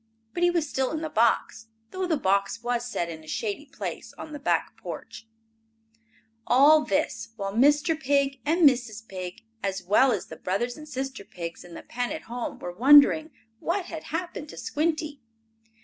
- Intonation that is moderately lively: No, wide, 6.5 semitones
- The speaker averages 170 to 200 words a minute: Yes, average, 180 wpm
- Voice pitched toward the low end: No, very high, 265 Hz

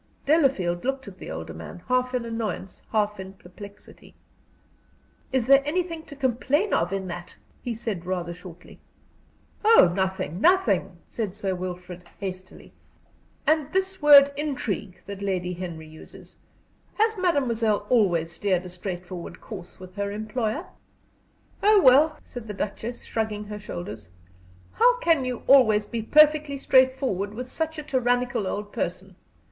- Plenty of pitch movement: Yes, wide, 6.6 semitones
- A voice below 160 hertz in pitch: No, high, 215 Hz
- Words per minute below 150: Yes, average, 140 wpm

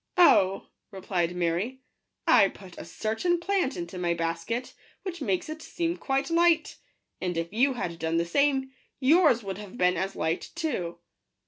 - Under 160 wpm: No, average, 175 wpm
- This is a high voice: Yes, high, 210 Hz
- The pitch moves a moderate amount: No, wide, 8.9 semitones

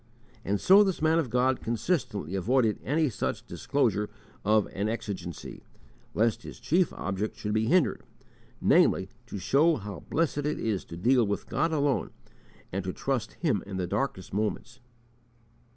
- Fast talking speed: No, average, 155 wpm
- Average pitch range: No, wide, 6.3 semitones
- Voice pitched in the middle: No, low, 115 Hz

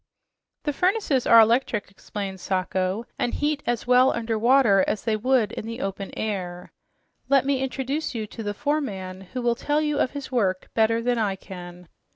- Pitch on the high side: Yes, high, 230 Hz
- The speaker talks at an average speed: Yes, average, 185 wpm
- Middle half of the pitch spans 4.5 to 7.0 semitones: Yes, average, 5.3 semitones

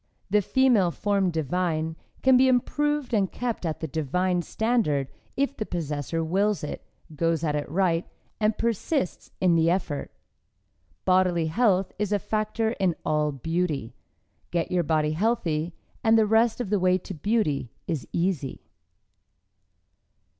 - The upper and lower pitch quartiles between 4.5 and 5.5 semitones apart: Yes, average, 5.1 semitones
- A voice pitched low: No, medium, 180 Hz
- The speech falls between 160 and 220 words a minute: No, average, 145 wpm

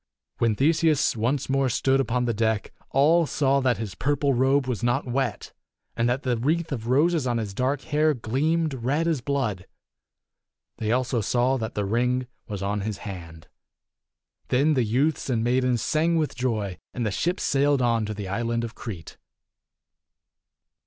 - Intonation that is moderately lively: Yes, average, 3.8 semitones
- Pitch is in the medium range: No, low, 125 Hz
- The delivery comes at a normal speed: Yes, average, 170 wpm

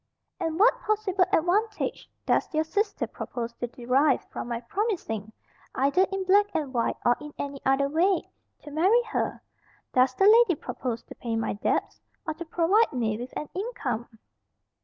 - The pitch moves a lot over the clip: Yes, wide, 8.0 semitones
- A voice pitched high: Yes, very high, 315 Hz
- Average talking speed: Yes, average, 165 wpm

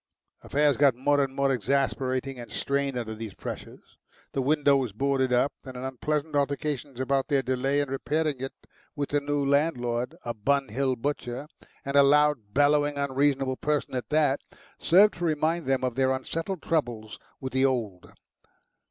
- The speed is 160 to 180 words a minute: Yes, average, 170 wpm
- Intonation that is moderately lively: No, narrow, 2.1 semitones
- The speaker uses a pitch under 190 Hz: Yes, medium, 140 Hz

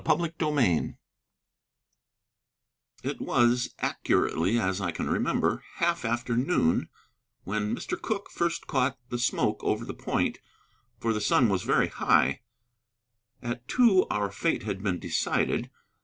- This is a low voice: Yes, low, 120 Hz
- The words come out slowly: Yes, slow, 130 wpm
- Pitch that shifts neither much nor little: No, wide, 6.7 semitones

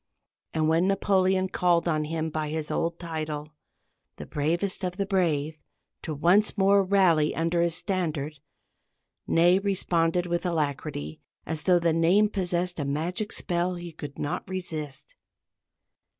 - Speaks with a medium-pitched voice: Yes, medium, 170 Hz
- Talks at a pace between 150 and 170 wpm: No, average, 140 wpm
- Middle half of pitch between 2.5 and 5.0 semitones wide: Yes, average, 3.0 semitones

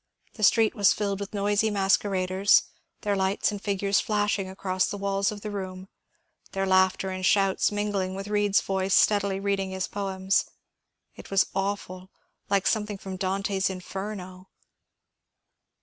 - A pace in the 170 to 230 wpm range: No, average, 150 wpm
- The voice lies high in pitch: Yes, high, 195 Hz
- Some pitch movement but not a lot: No, narrow, 1.3 semitones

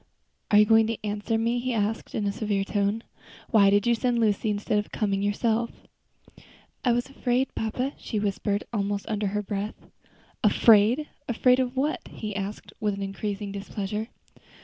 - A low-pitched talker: No, high, 210 Hz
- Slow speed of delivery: No, average, 165 wpm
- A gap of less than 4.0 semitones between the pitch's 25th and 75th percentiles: Yes, narrow, 2.4 semitones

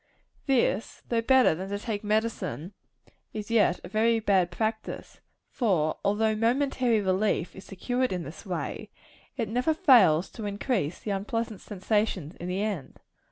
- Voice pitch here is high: Yes, high, 210 Hz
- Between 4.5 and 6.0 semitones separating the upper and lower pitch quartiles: No, average, 3.4 semitones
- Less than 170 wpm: Yes, average, 150 wpm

